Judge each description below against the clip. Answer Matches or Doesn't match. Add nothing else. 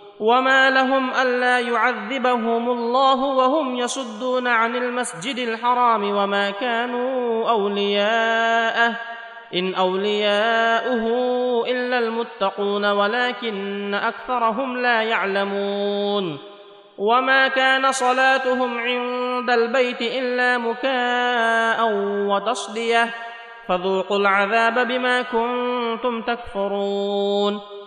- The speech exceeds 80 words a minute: Doesn't match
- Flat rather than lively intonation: Doesn't match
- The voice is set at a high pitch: Matches